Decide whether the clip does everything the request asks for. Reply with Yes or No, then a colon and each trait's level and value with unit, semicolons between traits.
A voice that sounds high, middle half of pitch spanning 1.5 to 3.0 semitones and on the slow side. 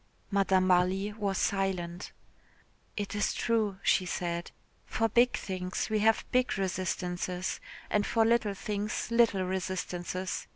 Yes: high, 195 Hz; narrow, 2.5 semitones; slow, 125 wpm